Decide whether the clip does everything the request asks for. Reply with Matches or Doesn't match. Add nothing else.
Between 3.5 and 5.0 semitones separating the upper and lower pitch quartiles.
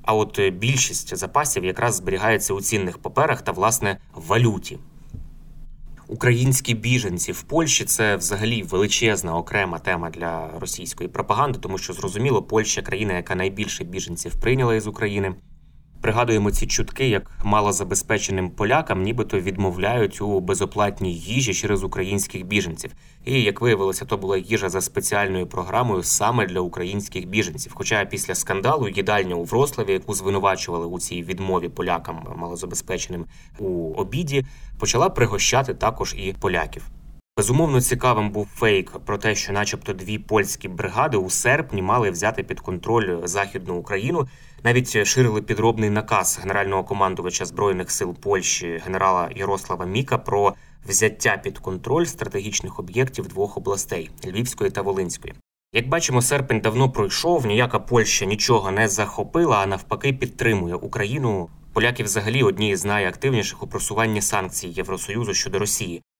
Matches